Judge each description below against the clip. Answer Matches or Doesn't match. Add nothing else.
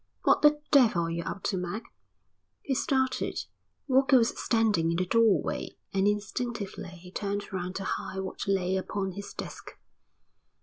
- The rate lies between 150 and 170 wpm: Matches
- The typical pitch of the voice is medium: Doesn't match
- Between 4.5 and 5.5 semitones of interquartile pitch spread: Doesn't match